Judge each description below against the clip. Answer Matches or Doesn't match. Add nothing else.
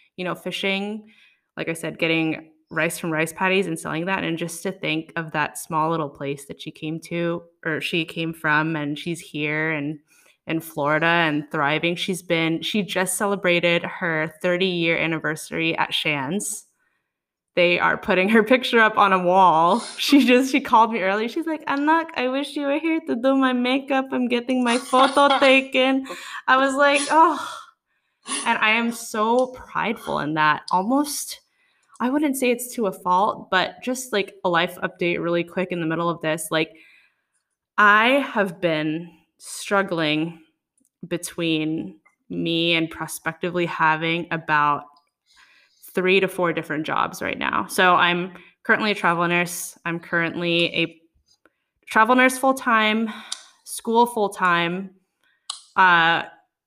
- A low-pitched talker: Doesn't match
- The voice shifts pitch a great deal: Matches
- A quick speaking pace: Doesn't match